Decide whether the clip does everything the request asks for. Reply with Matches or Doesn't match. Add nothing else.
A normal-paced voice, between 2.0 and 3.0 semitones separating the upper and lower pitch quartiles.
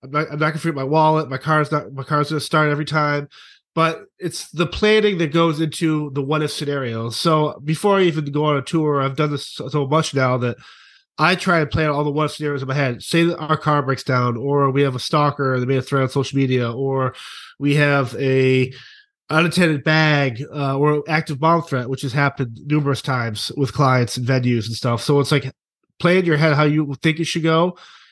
Doesn't match